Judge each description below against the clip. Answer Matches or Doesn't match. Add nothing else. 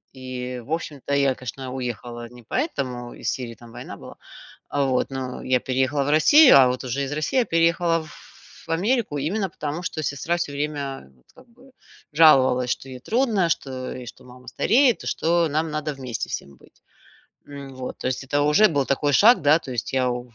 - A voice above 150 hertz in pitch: Doesn't match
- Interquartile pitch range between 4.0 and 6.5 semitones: Matches